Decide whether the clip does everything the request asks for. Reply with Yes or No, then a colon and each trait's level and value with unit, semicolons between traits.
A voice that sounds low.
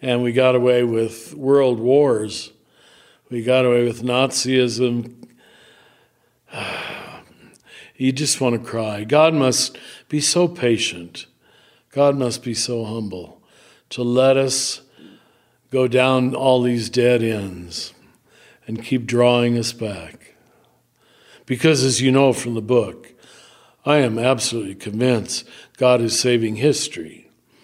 Yes: low, 125 Hz